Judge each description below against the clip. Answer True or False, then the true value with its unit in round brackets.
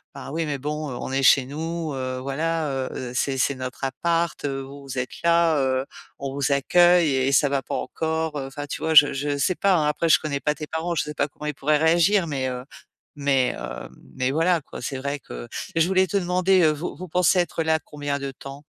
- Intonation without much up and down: False (3.3 semitones)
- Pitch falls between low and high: True (145 Hz)